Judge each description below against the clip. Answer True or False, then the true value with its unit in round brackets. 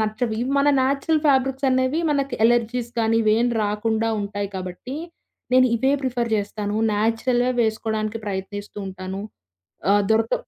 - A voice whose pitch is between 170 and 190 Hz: False (225 Hz)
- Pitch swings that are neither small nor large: True (3.6 semitones)